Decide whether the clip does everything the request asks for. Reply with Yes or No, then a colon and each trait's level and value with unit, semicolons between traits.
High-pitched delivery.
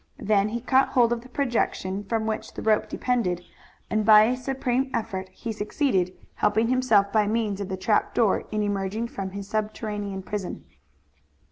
Yes: high, 215 Hz